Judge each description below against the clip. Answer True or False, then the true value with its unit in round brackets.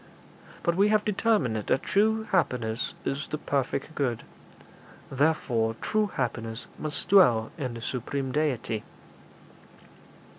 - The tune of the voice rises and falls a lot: True (7.8 semitones)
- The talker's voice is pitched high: False (140 Hz)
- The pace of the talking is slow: True (115 wpm)